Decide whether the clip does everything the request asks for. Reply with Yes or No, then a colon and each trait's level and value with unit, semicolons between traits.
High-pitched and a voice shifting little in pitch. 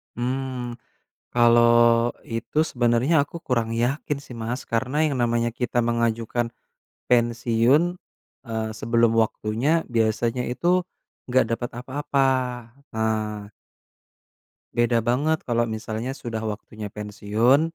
No: low, 120 Hz; narrow, 1.9 semitones